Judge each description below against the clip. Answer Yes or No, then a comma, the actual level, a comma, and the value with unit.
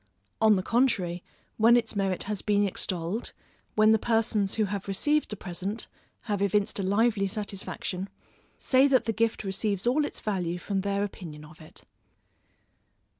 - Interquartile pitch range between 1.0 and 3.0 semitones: Yes, average, 2.7 semitones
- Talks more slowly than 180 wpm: Yes, average, 160 wpm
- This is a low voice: No, high, 205 Hz